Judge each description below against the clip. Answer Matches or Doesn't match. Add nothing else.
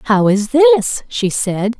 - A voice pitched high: Matches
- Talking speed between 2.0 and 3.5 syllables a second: Matches